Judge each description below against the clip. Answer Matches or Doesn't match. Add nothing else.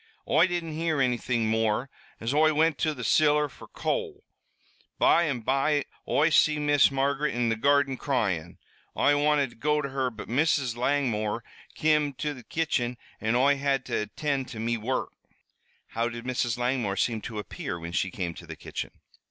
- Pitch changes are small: Doesn't match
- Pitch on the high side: Doesn't match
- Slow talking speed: Doesn't match